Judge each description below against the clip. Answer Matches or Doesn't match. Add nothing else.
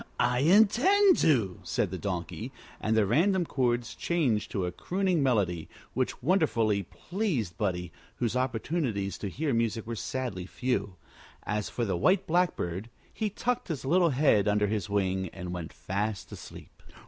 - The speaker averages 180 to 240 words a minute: Doesn't match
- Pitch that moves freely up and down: Matches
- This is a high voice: Doesn't match